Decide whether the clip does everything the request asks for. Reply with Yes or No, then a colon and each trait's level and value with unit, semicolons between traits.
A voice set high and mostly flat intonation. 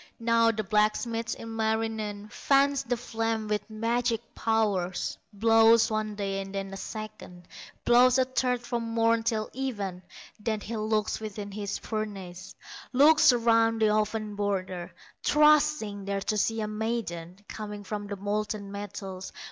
Yes: high, 215 Hz; narrow, 2.1 semitones